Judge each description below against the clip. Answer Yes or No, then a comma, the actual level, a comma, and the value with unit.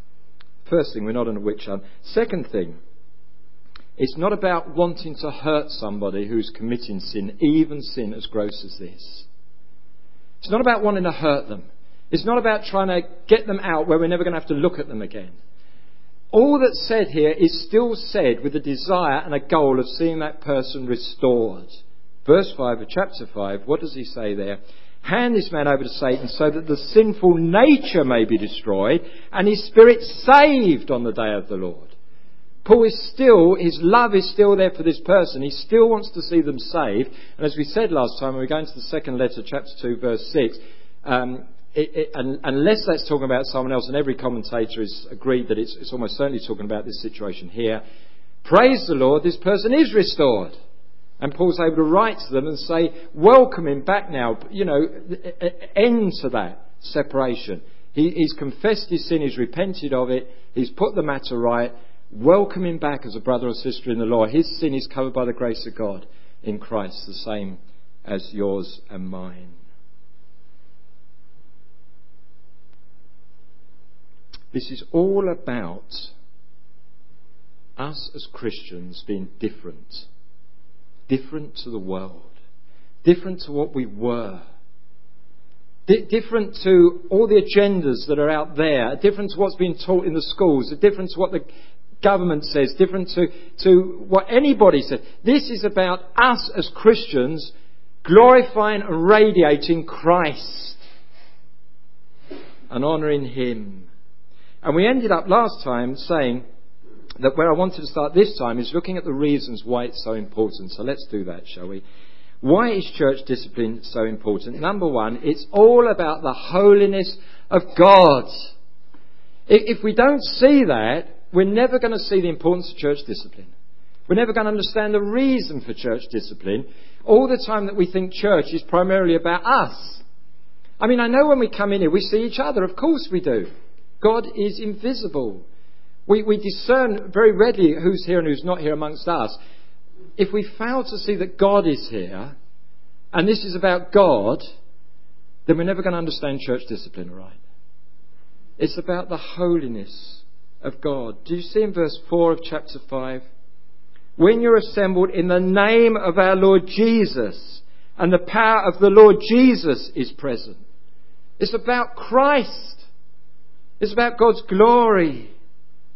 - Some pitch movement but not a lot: No, wide, 7.4 semitones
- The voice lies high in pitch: No, medium, 155 Hz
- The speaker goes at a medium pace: Yes, average, 170 wpm